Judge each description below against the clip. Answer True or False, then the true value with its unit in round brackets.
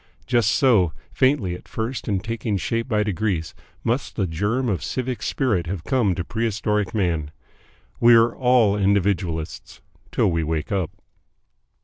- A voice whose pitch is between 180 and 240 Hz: False (105 Hz)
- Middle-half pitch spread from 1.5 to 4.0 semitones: False (4.5 semitones)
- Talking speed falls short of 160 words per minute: True (145 wpm)